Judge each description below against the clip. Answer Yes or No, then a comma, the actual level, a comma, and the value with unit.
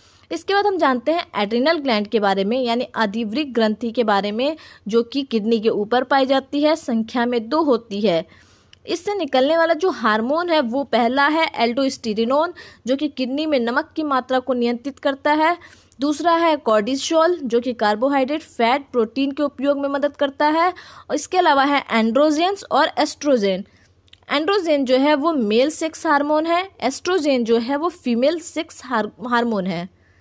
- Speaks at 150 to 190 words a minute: Yes, average, 170 wpm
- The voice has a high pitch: Yes, very high, 275 Hz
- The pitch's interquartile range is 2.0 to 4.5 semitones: No, average, 4.9 semitones